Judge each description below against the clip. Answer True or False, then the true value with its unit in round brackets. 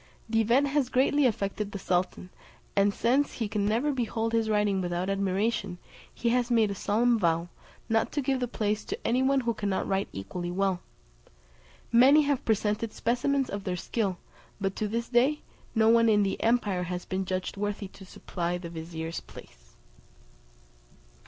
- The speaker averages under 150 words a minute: False (170 wpm)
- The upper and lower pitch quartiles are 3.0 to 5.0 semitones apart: True (4.0 semitones)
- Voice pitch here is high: True (210 Hz)